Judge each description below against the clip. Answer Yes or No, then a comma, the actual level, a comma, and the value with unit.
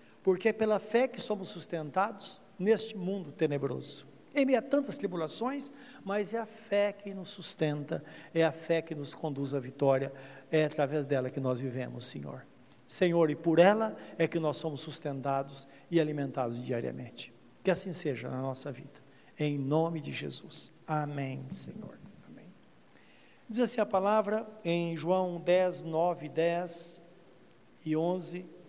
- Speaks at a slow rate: No, average, 155 wpm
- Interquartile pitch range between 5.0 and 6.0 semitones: Yes, wide, 5.5 semitones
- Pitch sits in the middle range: Yes, medium, 165 Hz